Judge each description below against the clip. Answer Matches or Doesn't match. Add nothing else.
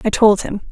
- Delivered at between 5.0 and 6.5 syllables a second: Matches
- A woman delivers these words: Matches